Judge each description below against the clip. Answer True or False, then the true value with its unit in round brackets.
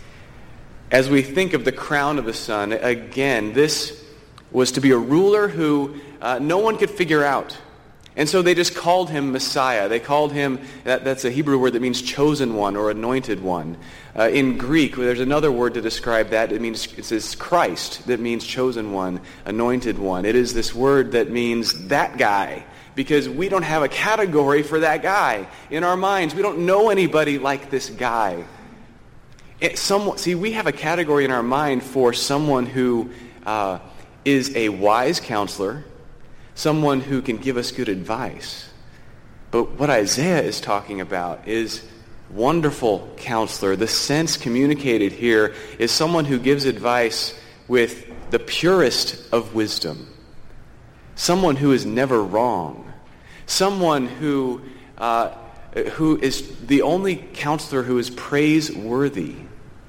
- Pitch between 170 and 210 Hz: False (130 Hz)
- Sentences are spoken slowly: False (155 wpm)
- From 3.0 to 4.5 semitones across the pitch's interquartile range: True (4.2 semitones)